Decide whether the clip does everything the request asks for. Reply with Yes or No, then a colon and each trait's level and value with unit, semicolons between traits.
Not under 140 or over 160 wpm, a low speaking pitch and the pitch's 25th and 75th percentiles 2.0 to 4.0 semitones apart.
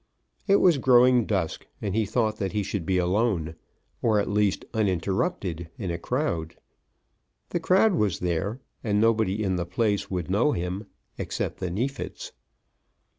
No: average, 155 wpm; low, 105 Hz; average, 4.7 semitones